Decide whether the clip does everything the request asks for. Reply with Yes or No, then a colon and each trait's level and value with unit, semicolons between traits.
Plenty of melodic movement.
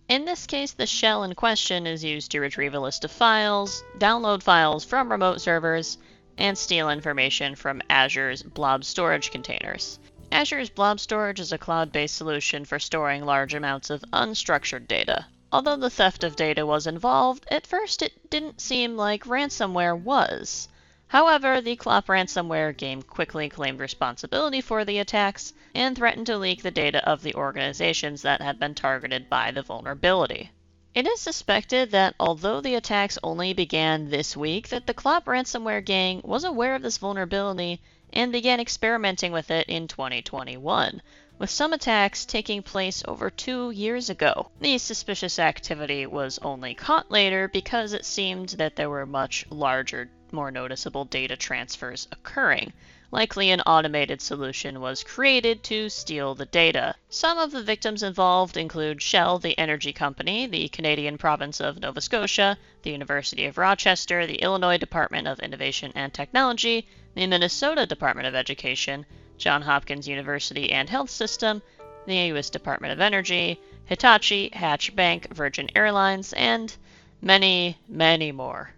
Yes: wide, 6.8 semitones